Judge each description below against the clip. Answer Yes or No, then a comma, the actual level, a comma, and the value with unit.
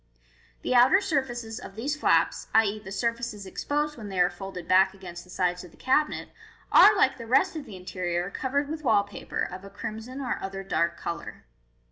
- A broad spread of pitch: Yes, wide, 5.9 semitones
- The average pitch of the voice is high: Yes, high, 215 Hz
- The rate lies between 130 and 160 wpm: No, average, 195 wpm